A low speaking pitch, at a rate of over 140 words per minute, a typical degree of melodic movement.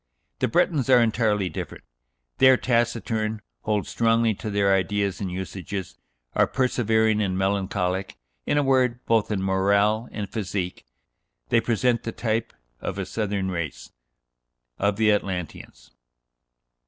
No: low, 105 Hz; slow, 135 wpm; average, 3.1 semitones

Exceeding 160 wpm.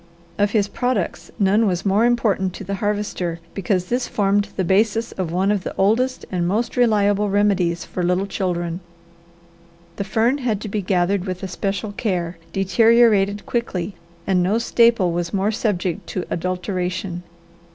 No: average, 155 wpm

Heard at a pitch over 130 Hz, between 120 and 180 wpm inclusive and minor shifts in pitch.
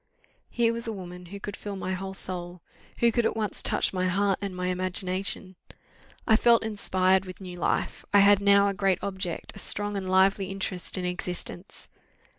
No: high, 190 Hz; average, 190 wpm; narrow, 1.7 semitones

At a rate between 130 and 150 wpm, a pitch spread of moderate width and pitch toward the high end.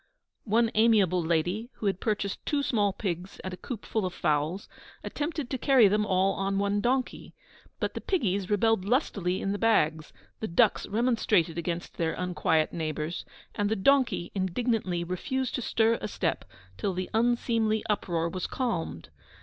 No: average, 165 wpm; average, 4.3 semitones; high, 200 Hz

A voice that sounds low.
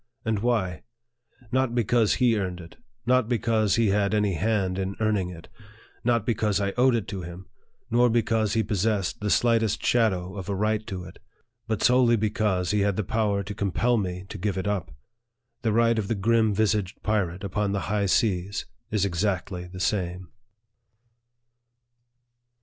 Yes: low, 105 Hz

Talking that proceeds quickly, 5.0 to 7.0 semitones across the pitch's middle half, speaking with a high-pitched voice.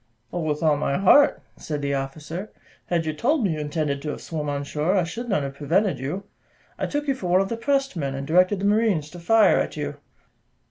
No: fast, 235 wpm; wide, 5.6 semitones; medium, 170 Hz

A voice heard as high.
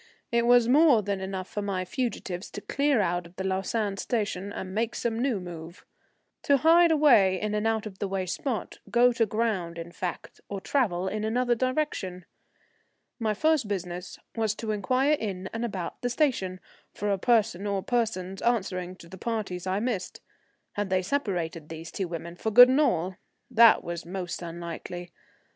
Yes: high, 205 Hz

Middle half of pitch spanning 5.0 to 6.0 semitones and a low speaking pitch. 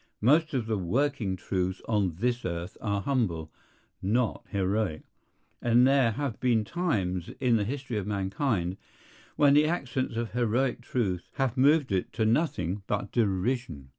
Yes: wide, 5.4 semitones; low, 115 Hz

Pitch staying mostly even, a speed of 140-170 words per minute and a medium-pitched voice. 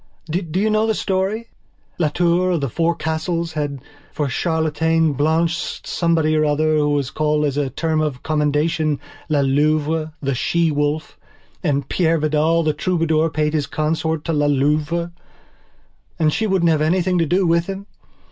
Yes: narrow, 2.1 semitones; average, 165 wpm; medium, 155 Hz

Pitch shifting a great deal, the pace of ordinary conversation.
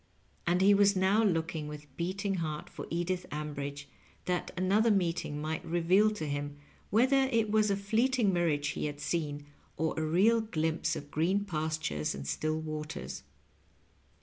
No: average, 4.8 semitones; average, 155 wpm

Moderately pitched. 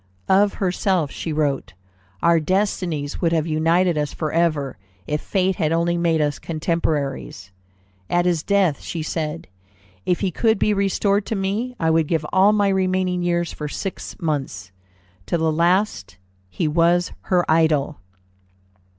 Yes: medium, 170 Hz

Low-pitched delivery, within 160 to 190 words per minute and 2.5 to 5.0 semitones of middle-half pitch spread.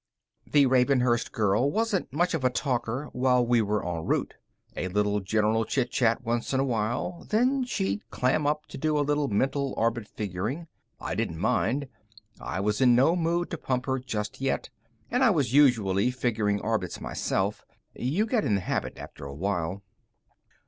No: low, 125 Hz; average, 175 wpm; wide, 5.5 semitones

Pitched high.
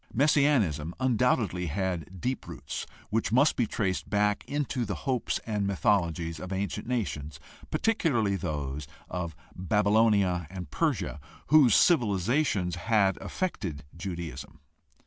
No: low, 100 Hz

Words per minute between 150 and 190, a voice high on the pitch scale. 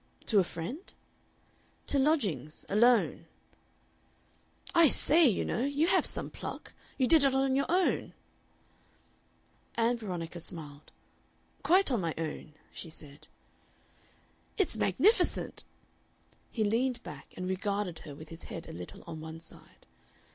No: slow, 135 wpm; high, 210 Hz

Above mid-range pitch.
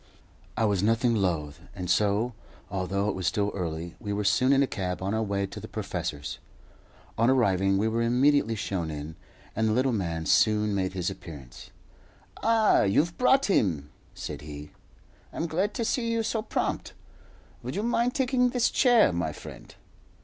No: low, 105 Hz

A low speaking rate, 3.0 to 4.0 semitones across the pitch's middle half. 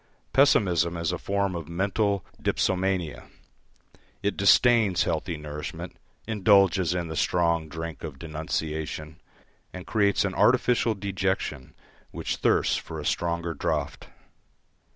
Yes: slow, 115 wpm; average, 3.5 semitones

